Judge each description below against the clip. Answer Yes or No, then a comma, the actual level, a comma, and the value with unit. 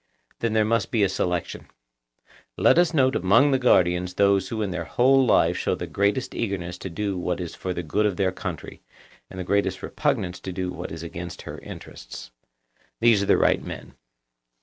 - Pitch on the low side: Yes, very low, 95 Hz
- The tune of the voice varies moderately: Yes, average, 4.2 semitones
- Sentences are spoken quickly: No, average, 195 wpm